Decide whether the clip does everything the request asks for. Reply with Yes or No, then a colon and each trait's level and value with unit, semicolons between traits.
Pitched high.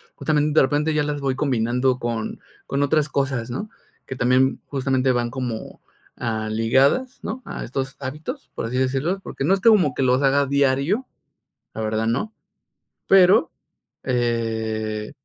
No: low, 130 Hz